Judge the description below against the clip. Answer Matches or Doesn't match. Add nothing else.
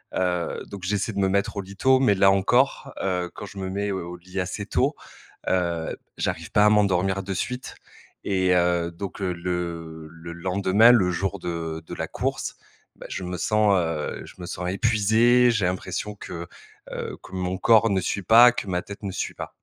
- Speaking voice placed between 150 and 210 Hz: Doesn't match